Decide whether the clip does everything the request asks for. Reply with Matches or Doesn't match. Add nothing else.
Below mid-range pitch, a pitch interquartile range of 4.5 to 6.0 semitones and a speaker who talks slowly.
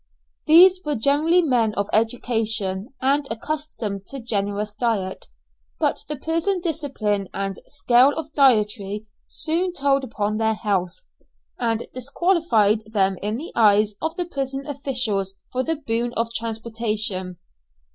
Doesn't match